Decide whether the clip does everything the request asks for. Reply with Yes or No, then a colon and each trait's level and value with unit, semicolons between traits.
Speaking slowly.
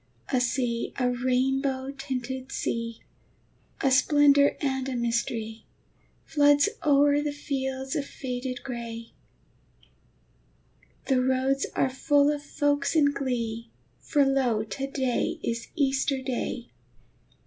Yes: slow, 115 wpm